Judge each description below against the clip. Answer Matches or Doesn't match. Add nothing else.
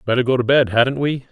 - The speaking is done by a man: Matches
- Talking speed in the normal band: Doesn't match